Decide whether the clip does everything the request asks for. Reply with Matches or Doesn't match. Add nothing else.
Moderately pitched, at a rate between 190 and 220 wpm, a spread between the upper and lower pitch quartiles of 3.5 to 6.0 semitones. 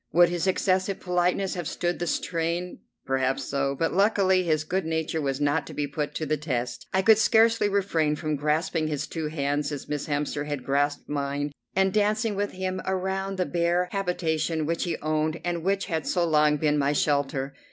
Matches